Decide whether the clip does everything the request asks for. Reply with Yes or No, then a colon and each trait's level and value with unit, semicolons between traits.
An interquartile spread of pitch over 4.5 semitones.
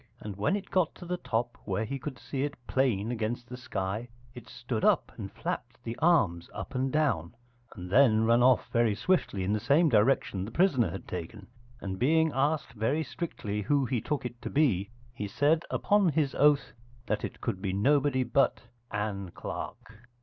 Yes: wide, 5.6 semitones